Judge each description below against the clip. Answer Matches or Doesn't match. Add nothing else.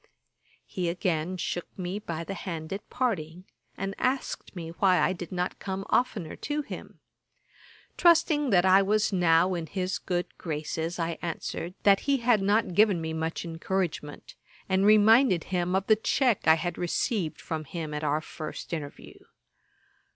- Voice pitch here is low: Doesn't match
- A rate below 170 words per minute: Matches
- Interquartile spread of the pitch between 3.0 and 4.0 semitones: Matches